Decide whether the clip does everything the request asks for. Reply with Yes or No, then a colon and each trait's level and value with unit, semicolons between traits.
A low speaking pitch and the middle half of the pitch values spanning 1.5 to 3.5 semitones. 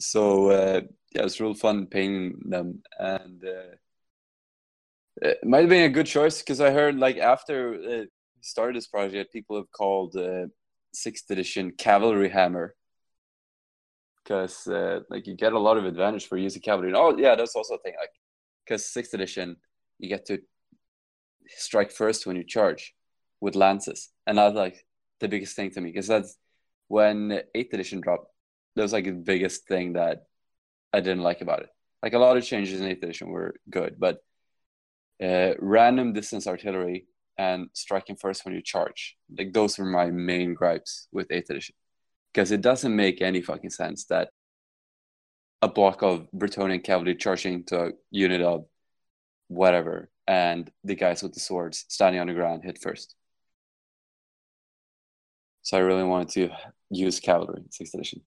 Yes: very low, 95 Hz; average, 2.8 semitones